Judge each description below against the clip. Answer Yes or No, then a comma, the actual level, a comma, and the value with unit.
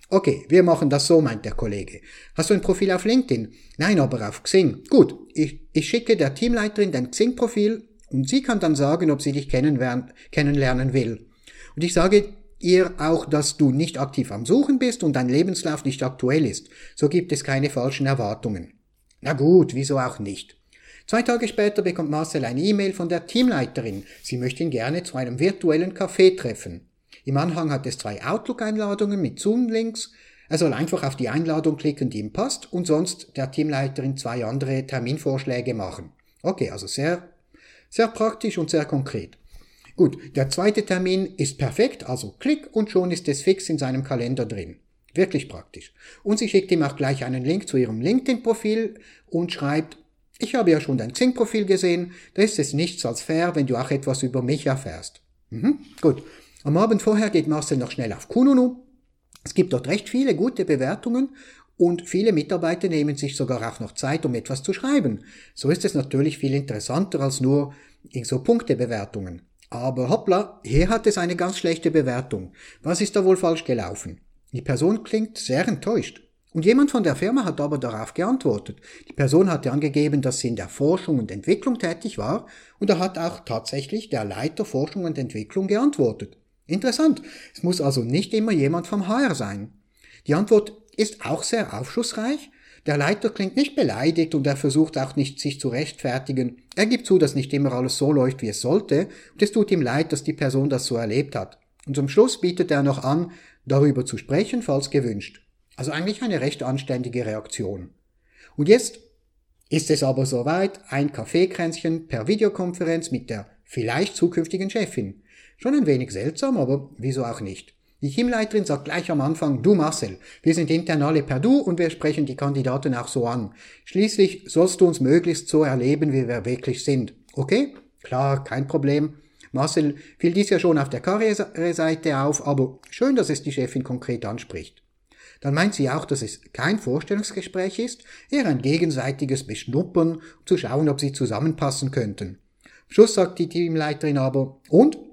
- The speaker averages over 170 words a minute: Yes, average, 180 wpm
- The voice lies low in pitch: No, medium, 155 Hz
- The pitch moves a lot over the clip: Yes, wide, 6.4 semitones